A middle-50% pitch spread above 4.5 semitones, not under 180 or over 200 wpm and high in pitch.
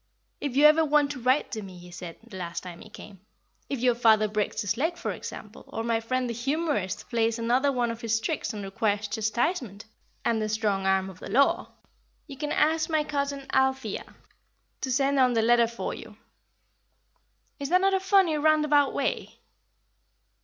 Yes: average, 5.0 semitones; average, 185 wpm; high, 240 Hz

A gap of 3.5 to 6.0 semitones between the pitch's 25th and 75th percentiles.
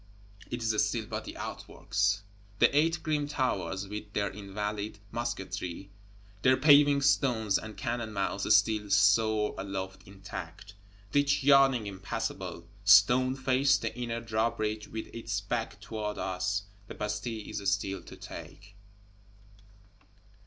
No: average, 3.1 semitones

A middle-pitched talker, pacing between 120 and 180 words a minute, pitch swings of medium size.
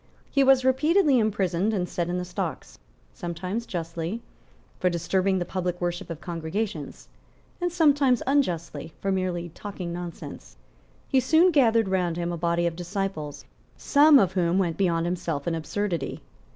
Yes: medium, 180 Hz; average, 150 wpm; average, 4.6 semitones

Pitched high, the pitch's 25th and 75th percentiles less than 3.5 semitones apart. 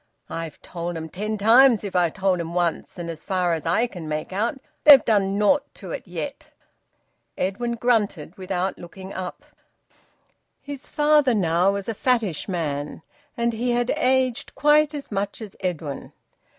No: high, 195 Hz; wide, 5.6 semitones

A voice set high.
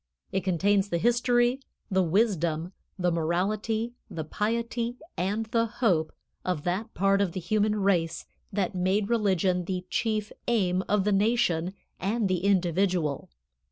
Yes: high, 195 Hz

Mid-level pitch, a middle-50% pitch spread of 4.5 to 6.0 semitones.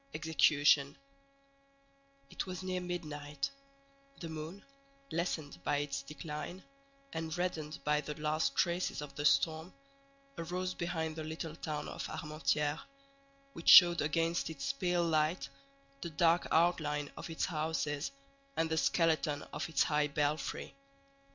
No: medium, 160 Hz; narrow, 2.4 semitones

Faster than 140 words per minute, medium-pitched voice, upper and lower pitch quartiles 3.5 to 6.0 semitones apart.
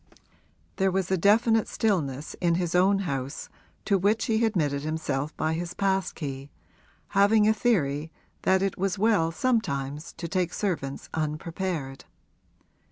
No: slow, 135 wpm; medium, 180 Hz; average, 4.7 semitones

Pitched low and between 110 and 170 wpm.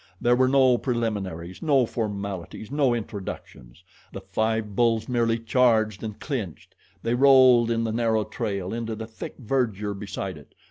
Yes: low, 115 Hz; average, 155 wpm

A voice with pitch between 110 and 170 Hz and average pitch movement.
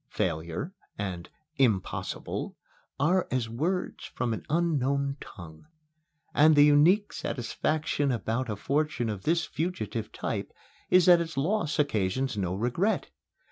No: medium, 140 Hz; wide, 6.5 semitones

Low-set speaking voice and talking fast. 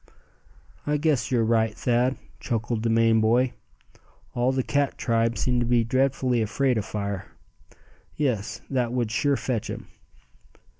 No: low, 120 Hz; average, 145 wpm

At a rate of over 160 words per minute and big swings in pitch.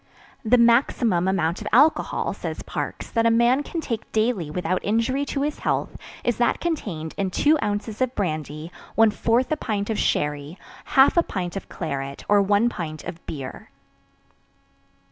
No: average, 150 wpm; wide, 5.8 semitones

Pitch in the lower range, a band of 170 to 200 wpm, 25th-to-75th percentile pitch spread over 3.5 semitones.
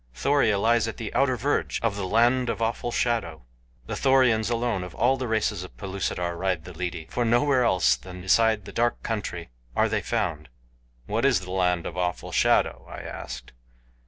Yes: low, 110 Hz; average, 190 wpm; average, 4.7 semitones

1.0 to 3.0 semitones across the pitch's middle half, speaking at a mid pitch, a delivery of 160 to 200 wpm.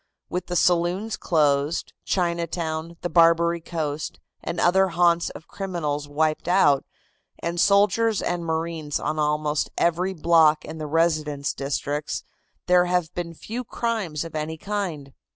No: narrow, 2.6 semitones; medium, 170 Hz; slow, 135 wpm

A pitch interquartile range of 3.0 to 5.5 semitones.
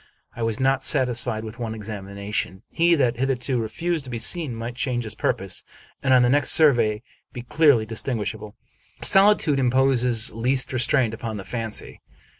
Yes: average, 3.3 semitones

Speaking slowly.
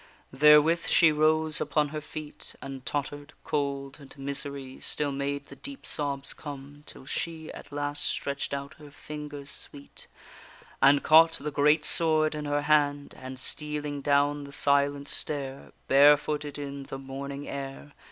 No: average, 150 wpm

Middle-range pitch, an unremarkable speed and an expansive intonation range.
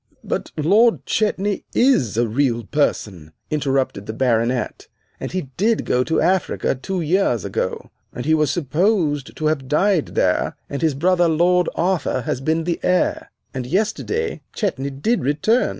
Yes: medium, 155 Hz; average, 155 wpm; wide, 5.9 semitones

